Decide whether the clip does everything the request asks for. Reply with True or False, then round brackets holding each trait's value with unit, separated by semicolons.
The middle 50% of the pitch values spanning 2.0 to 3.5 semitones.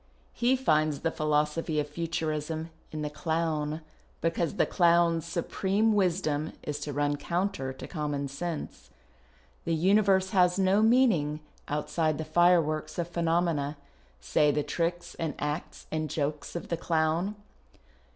True (2.7 semitones)